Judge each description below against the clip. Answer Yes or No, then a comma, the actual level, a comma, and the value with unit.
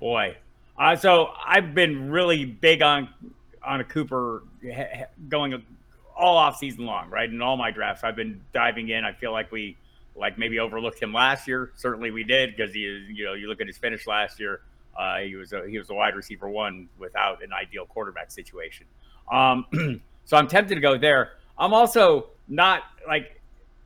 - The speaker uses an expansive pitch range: Yes, wide, 5.8 semitones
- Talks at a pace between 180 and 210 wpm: Yes, average, 200 wpm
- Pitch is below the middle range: Yes, low, 130 Hz